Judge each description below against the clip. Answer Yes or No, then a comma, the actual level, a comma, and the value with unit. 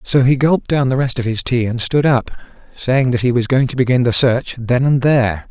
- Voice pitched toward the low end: Yes, low, 125 Hz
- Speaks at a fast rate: Yes, fast, 260 wpm